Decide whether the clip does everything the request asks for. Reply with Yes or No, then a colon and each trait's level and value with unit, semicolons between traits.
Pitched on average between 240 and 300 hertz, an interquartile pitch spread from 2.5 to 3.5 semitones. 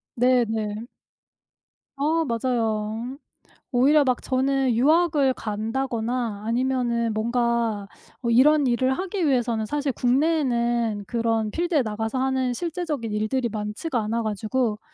Yes: high, 245 Hz; average, 3.1 semitones